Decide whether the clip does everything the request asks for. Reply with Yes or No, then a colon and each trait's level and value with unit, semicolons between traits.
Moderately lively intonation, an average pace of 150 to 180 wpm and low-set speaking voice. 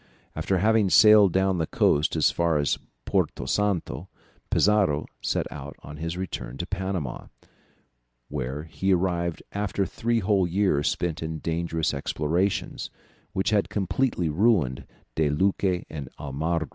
No: average, 4.4 semitones; slow, 135 wpm; very low, 85 Hz